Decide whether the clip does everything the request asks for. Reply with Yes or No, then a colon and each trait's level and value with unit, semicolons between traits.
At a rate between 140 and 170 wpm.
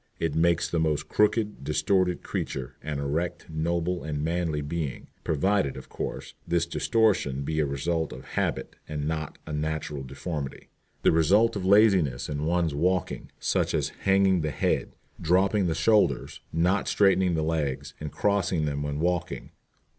Yes: average, 155 wpm